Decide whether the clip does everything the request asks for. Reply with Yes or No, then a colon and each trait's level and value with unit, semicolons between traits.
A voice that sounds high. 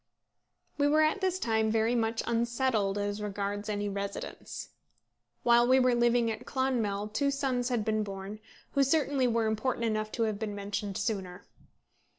Yes: high, 225 Hz